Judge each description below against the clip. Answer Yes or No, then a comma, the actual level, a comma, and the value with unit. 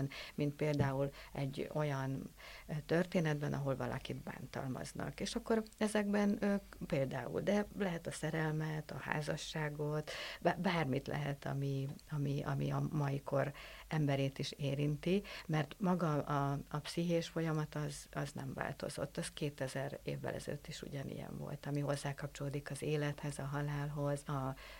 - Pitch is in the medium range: Yes, medium, 150 Hz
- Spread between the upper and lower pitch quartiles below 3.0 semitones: Yes, narrow, 2.5 semitones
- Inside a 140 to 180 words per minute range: No, average, 130 wpm